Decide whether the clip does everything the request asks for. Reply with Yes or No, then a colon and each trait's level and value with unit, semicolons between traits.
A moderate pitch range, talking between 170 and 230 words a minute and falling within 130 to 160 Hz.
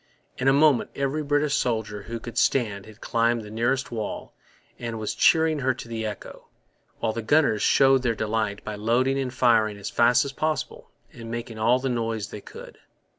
No: average, 3.5 semitones; average, 190 wpm; low, 115 Hz